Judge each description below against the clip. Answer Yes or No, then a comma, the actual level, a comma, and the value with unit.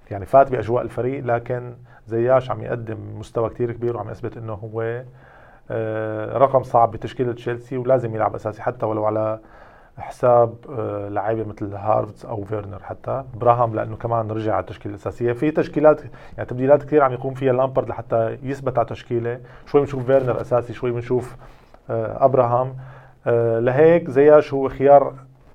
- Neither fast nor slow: No, fast, 150 wpm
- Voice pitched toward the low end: Yes, low, 120 Hz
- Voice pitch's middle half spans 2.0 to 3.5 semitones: Yes, average, 2.9 semitones